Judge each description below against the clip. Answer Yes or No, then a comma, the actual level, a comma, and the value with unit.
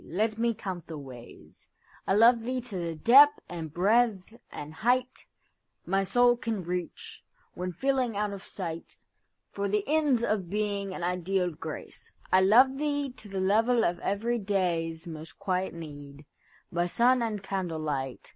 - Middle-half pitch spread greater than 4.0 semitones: Yes, average, 5.3 semitones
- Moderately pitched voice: No, high, 195 Hz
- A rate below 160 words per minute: Yes, average, 145 wpm